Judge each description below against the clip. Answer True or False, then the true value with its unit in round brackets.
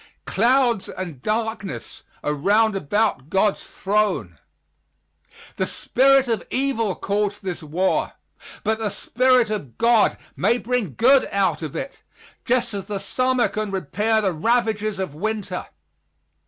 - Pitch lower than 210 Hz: False (215 Hz)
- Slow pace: True (130 wpm)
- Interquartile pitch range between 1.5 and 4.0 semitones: True (3.5 semitones)